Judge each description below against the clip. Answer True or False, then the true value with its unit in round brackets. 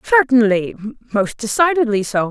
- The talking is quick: False (105 wpm)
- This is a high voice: True (235 Hz)